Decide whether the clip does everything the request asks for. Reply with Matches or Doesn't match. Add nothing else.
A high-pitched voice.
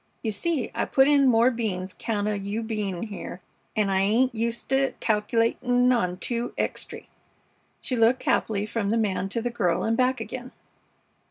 Matches